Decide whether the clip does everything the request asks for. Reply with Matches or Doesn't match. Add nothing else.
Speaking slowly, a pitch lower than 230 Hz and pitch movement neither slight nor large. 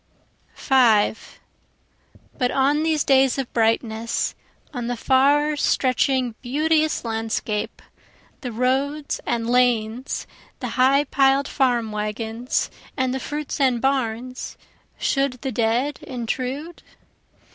Doesn't match